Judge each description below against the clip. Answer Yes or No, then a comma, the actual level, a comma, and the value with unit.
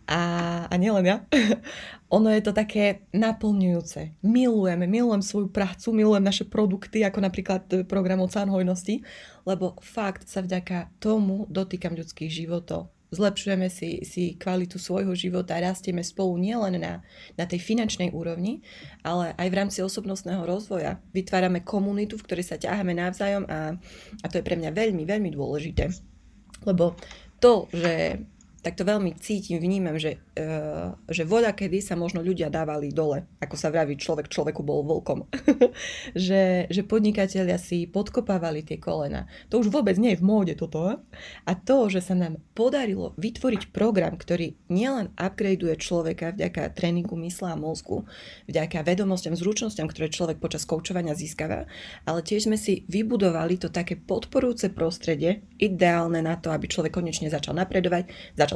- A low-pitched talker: No, medium, 185 Hz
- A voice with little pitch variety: No, average, 3.3 semitones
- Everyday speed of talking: Yes, average, 150 wpm